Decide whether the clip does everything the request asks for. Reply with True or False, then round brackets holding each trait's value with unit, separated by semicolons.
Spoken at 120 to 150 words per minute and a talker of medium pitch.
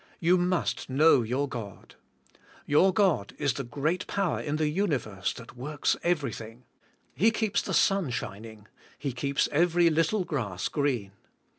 True (145 wpm; 145 Hz)